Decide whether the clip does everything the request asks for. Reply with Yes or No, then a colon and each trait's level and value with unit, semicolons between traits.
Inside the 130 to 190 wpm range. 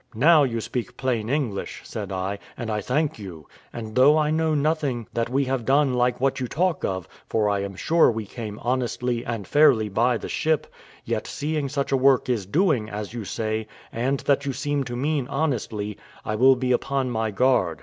No: average, 200 wpm